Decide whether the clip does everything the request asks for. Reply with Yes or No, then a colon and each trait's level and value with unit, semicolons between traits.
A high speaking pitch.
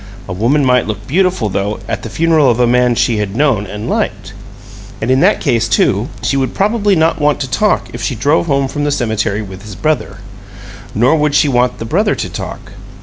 No: low, 125 Hz